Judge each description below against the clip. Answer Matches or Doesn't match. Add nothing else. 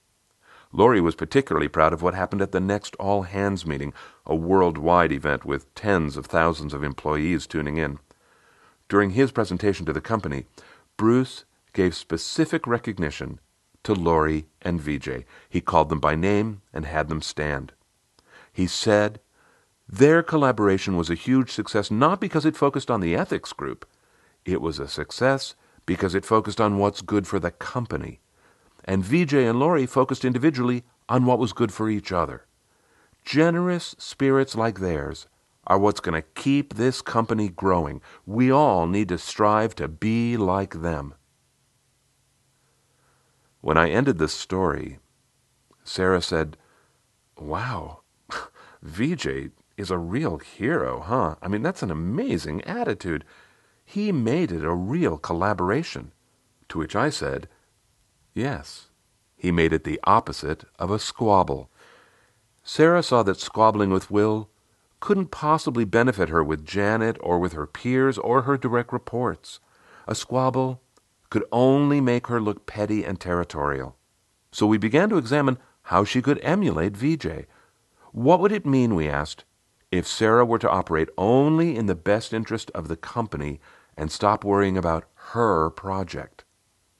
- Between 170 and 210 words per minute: Doesn't match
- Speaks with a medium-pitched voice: Doesn't match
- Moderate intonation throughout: Doesn't match